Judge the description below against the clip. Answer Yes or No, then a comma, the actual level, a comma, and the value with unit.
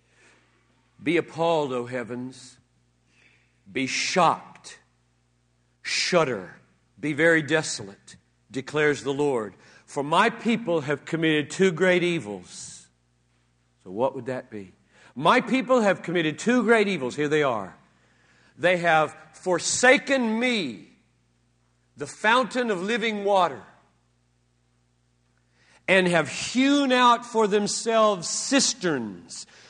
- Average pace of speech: No, slow, 105 wpm